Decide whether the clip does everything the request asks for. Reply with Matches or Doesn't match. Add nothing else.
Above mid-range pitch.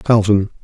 Doesn't match